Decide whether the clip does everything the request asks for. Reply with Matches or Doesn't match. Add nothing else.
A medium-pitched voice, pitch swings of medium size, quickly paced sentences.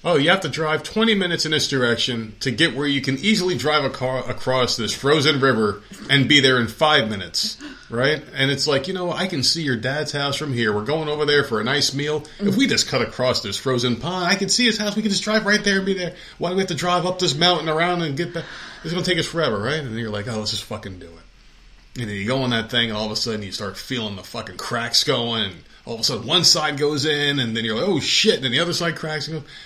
Doesn't match